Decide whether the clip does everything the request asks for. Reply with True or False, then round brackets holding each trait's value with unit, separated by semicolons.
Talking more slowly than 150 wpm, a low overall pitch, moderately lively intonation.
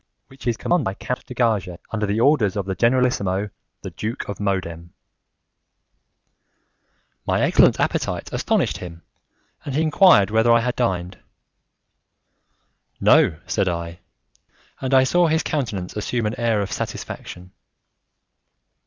True (135 wpm; 110 Hz; 5.0 semitones)